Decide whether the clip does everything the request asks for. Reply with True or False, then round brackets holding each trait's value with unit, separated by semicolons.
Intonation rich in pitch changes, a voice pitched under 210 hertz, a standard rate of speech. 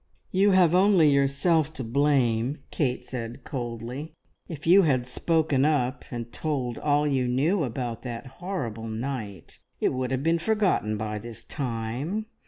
False (5.0 semitones; 135 Hz; 150 wpm)